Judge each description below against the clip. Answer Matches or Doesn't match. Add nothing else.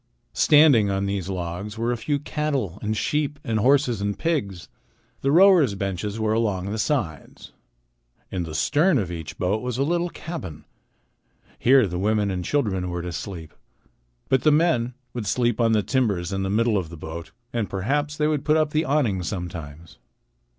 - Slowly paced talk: Doesn't match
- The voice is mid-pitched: Doesn't match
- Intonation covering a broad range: Matches